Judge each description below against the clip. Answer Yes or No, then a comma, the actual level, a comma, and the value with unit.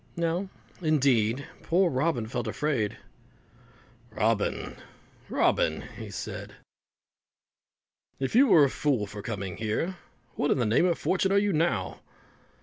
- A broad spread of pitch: Yes, wide, 7.5 semitones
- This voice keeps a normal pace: No, slow, 130 wpm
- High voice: No, medium, 140 Hz